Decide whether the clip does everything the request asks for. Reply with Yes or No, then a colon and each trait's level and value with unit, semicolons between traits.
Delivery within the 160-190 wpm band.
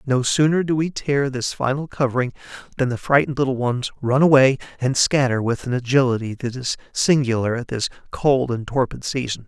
Yes: average, 185 wpm